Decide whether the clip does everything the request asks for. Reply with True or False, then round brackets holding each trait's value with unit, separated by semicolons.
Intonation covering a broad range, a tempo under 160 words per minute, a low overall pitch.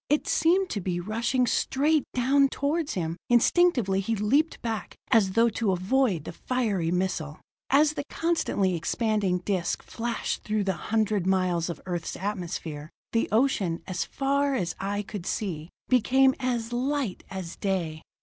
False (6.2 semitones; 150 wpm; 210 Hz)